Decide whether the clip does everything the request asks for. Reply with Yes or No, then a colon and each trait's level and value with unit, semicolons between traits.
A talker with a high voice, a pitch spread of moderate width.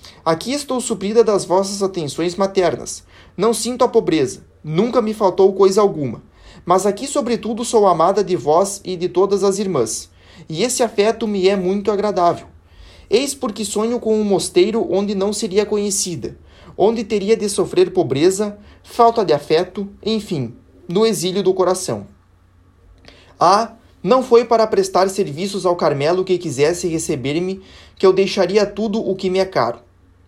Yes: high, 195 Hz; average, 4.1 semitones